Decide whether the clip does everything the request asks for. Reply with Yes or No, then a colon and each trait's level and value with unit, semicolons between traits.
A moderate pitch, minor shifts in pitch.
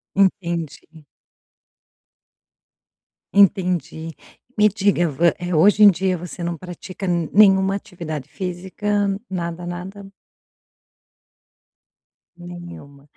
Yes: medium, 180 Hz; narrow, 2.3 semitones